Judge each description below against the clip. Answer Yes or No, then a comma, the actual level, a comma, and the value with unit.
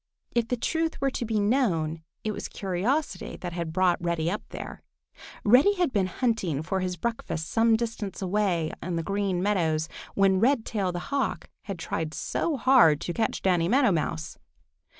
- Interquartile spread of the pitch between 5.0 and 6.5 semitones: Yes, wide, 5.4 semitones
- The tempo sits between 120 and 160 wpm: No, average, 170 wpm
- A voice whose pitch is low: No, high, 195 Hz